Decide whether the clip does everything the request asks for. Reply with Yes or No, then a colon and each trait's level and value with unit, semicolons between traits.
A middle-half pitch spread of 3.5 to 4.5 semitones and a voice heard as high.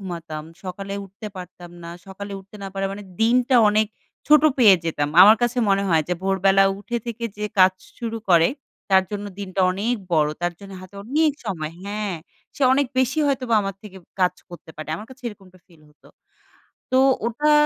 Yes: average, 4.0 semitones; high, 195 Hz